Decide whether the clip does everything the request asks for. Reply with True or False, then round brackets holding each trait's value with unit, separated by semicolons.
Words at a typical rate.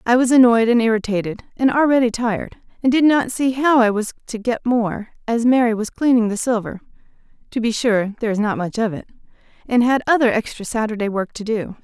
False (210 wpm)